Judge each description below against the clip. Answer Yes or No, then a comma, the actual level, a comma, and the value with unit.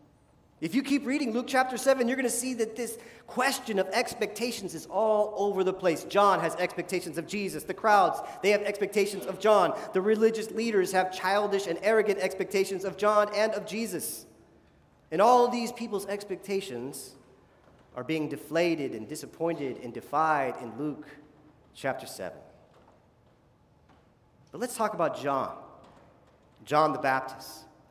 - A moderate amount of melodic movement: No, wide, 5.8 semitones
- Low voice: No, high, 195 Hz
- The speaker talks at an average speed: Yes, average, 150 wpm